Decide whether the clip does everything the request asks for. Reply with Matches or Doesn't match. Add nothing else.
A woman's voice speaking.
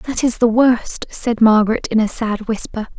Matches